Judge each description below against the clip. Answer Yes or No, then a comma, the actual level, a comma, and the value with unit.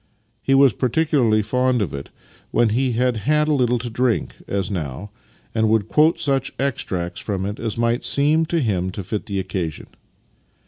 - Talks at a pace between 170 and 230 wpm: Yes, average, 195 wpm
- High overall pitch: No, low, 115 Hz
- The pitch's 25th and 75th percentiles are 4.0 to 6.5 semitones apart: Yes, average, 5.1 semitones